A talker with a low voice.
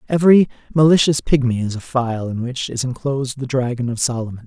Yes: low, 130 Hz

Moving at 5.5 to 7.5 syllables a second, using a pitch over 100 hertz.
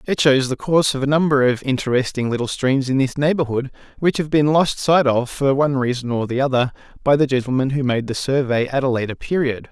Yes: 5.9 syllables/s; low, 135 Hz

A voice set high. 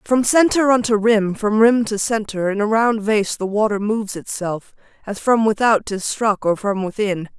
Yes: high, 210 Hz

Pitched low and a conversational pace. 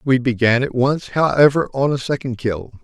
Yes: low, 130 Hz; average, 190 wpm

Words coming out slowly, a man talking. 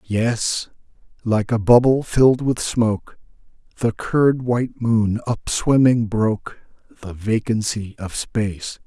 Yes: slow, 110 wpm; male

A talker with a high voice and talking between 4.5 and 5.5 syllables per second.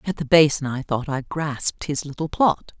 No: medium, 145 Hz; 4.9 syllables/s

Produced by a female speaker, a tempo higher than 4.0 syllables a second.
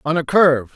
No: male; 6.2 syllables/s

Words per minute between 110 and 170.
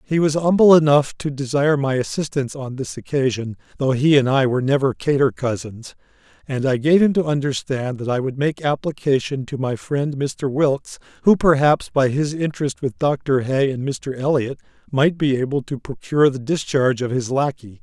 No: average, 190 wpm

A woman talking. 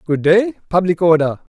No: male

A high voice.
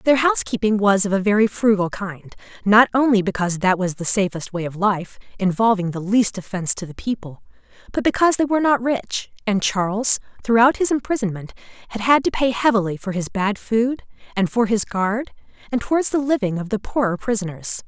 Yes: high, 215 Hz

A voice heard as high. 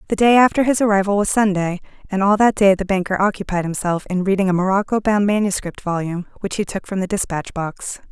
Yes: high, 195 Hz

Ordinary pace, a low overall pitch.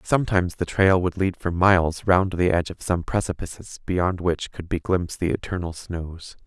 Yes: average, 195 wpm; very low, 90 Hz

